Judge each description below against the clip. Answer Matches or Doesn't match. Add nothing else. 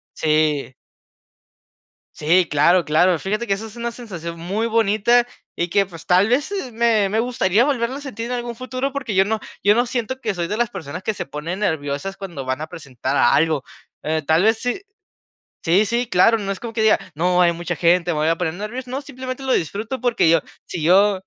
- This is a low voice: Doesn't match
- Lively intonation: Matches